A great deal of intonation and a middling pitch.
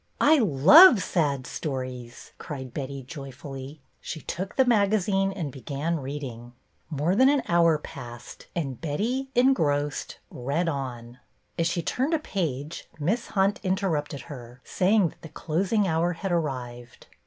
Yes: wide, 6.2 semitones; medium, 160 Hz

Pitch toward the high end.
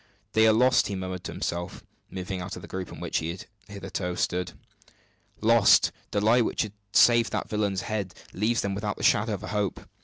No: low, 100 Hz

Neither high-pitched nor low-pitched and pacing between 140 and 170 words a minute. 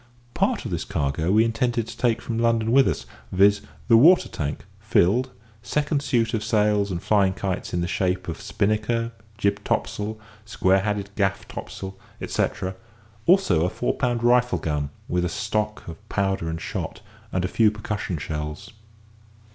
No: low, 105 Hz; average, 165 wpm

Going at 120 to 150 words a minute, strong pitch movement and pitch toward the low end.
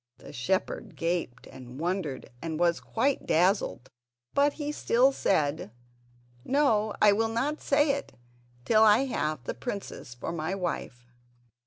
No: average, 145 wpm; wide, 7.3 semitones; high, 190 Hz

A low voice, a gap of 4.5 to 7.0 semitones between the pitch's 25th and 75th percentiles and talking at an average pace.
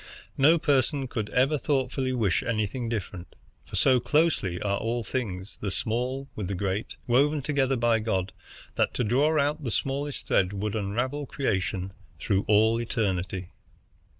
Yes: low, 115 Hz; average, 5.1 semitones; average, 150 wpm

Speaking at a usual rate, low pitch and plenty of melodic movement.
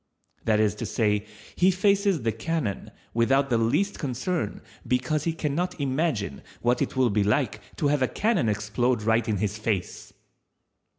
Yes: average, 170 wpm; low, 125 Hz; wide, 6.3 semitones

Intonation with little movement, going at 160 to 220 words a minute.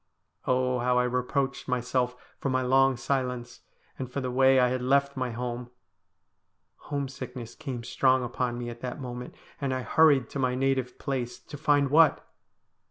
Yes: narrow, 1.4 semitones; average, 170 wpm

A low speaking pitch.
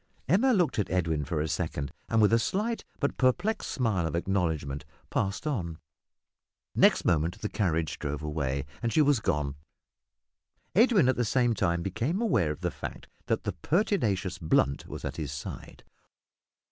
Yes: very low, 95 Hz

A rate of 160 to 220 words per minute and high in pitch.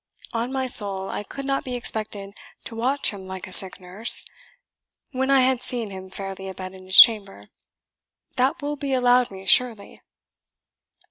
Yes: average, 175 wpm; high, 220 Hz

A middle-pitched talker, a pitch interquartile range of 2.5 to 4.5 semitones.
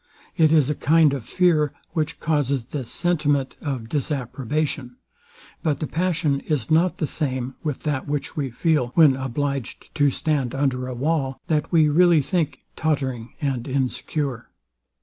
Yes: medium, 145 Hz; average, 3.0 semitones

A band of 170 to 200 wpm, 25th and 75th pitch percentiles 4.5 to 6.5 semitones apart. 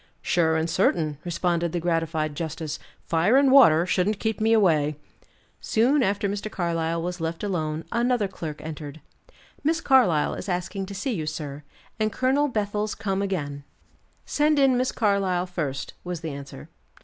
No: average, 160 wpm; average, 5.1 semitones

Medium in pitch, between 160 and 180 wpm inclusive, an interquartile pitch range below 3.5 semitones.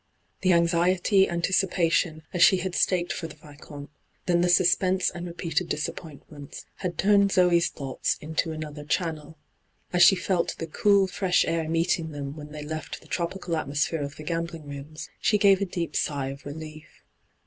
Yes: medium, 165 Hz; average, 170 wpm; average, 2.9 semitones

